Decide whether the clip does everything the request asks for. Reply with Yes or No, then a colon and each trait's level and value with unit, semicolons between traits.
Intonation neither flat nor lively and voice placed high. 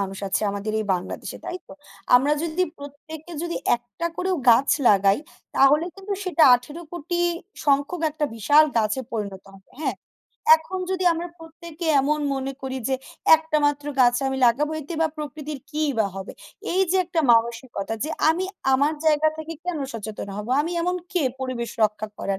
No: wide, 5.7 semitones; very high, 290 Hz